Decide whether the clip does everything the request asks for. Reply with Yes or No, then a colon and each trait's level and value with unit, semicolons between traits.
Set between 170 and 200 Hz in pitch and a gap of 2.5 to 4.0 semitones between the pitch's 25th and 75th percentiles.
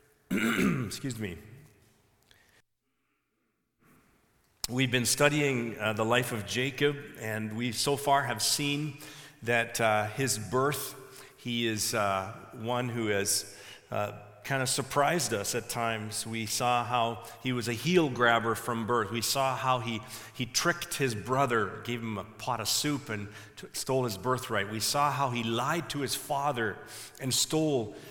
No: low, 120 Hz; average, 3.5 semitones